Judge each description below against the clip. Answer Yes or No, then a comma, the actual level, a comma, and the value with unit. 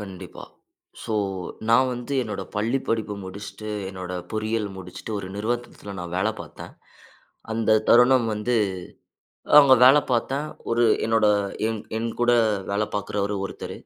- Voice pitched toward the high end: No, low, 110 Hz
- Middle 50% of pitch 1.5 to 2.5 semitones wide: No, average, 2.9 semitones